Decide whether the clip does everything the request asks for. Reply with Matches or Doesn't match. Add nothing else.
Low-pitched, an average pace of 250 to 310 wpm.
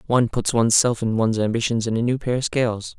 Matches